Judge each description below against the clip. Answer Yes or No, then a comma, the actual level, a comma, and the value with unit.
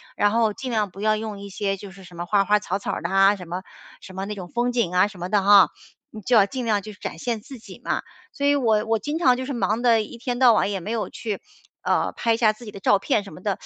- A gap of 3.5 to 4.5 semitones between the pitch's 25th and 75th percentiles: No, average, 3.0 semitones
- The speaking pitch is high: Yes, high, 210 Hz